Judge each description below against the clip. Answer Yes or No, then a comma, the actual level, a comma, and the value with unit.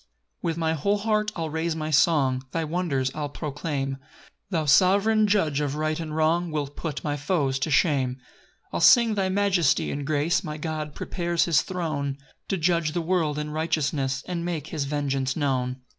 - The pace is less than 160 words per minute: No, average, 185 wpm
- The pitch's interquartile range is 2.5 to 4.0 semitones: Yes, average, 3.2 semitones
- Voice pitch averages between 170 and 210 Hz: No, medium, 155 Hz